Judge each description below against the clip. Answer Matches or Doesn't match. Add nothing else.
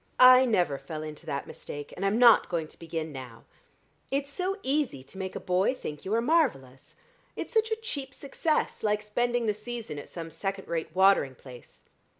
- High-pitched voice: Matches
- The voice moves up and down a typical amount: Doesn't match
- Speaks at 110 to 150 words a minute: Doesn't match